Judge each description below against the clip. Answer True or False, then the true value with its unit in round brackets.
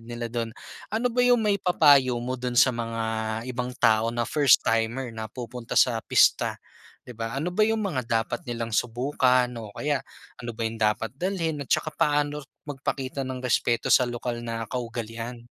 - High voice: False (125 Hz)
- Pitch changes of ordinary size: True (3.6 semitones)